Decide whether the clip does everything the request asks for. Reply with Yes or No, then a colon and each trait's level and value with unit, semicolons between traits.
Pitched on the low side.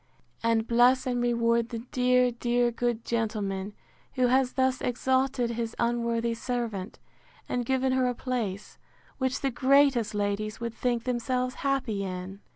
No: high, 240 Hz